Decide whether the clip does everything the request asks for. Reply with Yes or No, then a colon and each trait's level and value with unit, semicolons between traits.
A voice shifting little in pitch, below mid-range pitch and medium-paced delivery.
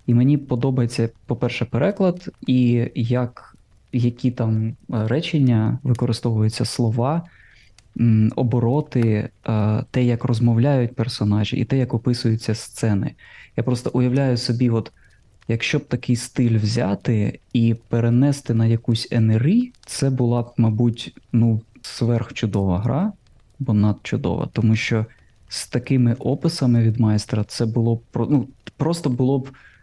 Yes: narrow, 2.2 semitones; low, 120 Hz; average, 120 wpm